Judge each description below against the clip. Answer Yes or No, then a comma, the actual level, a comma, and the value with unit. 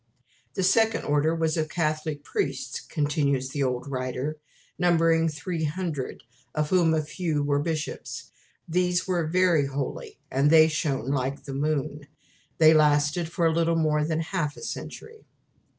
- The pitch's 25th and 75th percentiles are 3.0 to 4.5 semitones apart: No, narrow, 2.5 semitones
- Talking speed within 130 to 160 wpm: Yes, average, 150 wpm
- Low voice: No, medium, 155 Hz